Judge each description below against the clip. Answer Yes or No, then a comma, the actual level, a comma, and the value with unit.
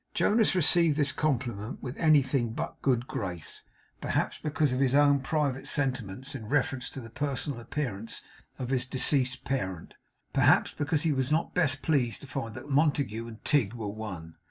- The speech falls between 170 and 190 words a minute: Yes, average, 175 wpm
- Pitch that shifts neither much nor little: Yes, average, 3.8 semitones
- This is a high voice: No, low, 135 Hz